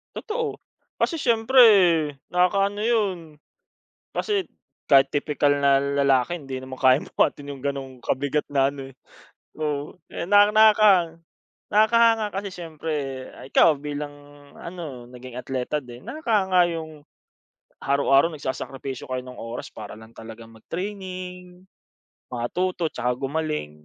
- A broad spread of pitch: Yes, wide, 6.0 semitones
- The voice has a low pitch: No, medium, 150 Hz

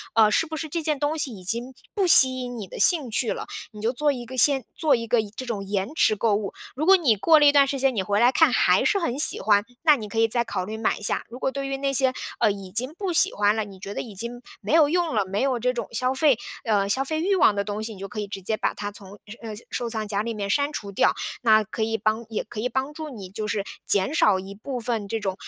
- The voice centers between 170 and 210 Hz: No, high, 230 Hz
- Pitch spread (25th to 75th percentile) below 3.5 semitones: No, average, 4.7 semitones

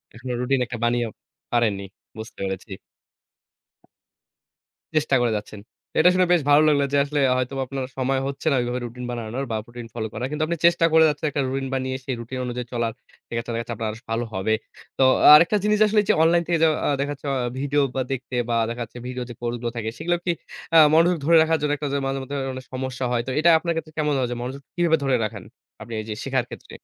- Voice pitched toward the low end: Yes, low, 130 Hz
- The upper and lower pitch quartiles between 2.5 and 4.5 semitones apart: Yes, average, 4.1 semitones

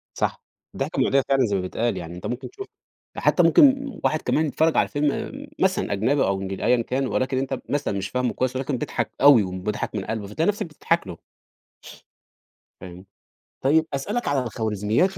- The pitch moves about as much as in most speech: No, wide, 6.1 semitones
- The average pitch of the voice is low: Yes, low, 125 Hz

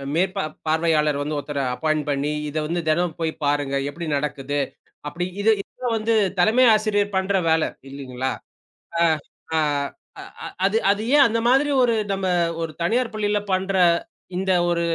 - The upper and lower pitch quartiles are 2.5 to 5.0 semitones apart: No, wide, 5.5 semitones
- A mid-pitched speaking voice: Yes, medium, 170 Hz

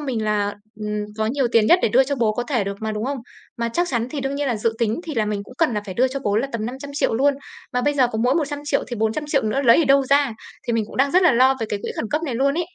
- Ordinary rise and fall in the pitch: Yes, average, 4.3 semitones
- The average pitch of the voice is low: No, very high, 250 Hz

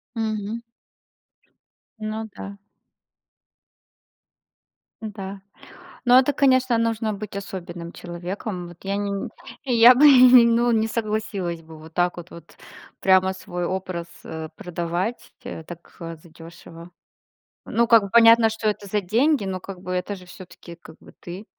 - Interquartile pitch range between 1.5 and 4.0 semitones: No, average, 4.4 semitones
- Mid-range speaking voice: No, high, 195 Hz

